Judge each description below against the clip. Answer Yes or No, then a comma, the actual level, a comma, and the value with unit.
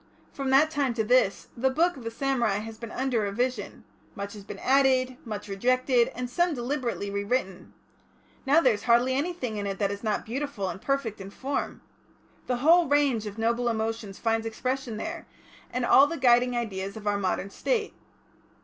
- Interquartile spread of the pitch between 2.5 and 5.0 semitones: Yes, average, 4.1 semitones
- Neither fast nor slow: Yes, average, 185 wpm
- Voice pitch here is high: Yes, high, 240 Hz